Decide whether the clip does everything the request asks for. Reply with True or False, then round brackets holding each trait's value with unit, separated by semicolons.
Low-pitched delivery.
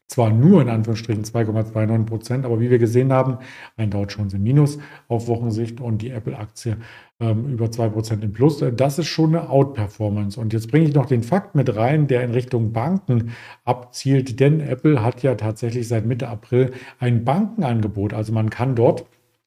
True (120 Hz)